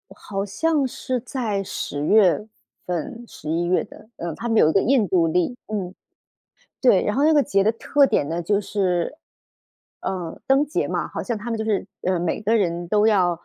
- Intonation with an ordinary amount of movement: Yes, average, 4.9 semitones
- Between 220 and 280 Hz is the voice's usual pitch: No, high, 205 Hz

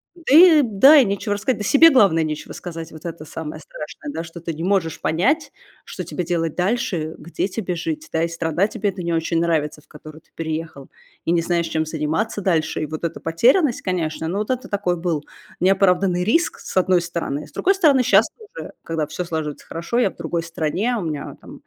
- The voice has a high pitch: No, medium, 175 Hz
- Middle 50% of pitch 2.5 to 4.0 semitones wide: No, average, 4.8 semitones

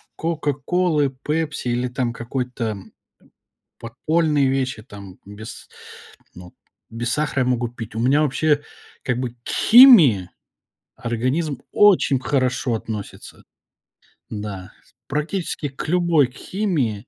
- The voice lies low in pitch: Yes, low, 130 Hz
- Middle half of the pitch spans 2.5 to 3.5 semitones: No, average, 4.6 semitones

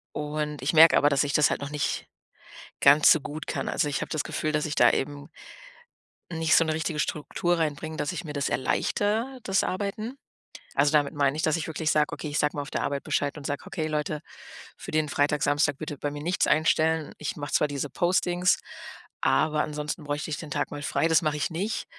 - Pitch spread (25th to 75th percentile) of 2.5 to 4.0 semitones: No, narrow, 1.8 semitones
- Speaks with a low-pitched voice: No, medium, 150 Hz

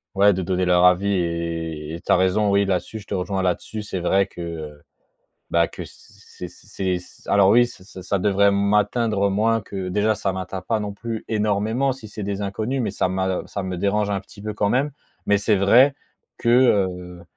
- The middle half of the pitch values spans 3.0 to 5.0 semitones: No, narrow, 2.5 semitones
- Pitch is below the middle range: Yes, low, 100 Hz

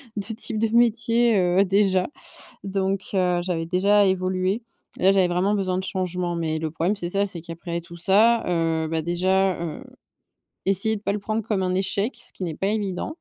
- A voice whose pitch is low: No, high, 190 Hz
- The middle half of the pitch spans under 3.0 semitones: Yes, narrow, 2.6 semitones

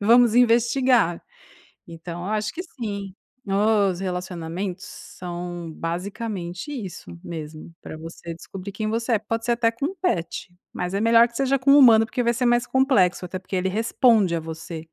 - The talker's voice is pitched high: Yes, high, 200 Hz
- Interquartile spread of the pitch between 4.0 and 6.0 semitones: Yes, average, 5.1 semitones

